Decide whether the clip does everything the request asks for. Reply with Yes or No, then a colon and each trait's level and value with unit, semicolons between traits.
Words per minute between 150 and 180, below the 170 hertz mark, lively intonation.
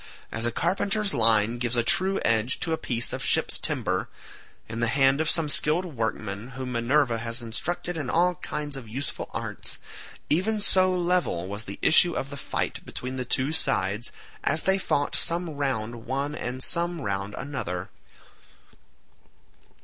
Yes: average, 160 wpm; low, 135 Hz; wide, 6.2 semitones